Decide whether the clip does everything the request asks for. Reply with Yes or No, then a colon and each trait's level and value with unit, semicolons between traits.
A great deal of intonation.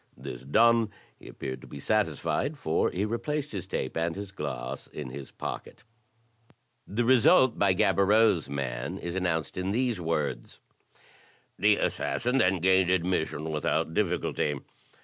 Yes: wide, 5.9 semitones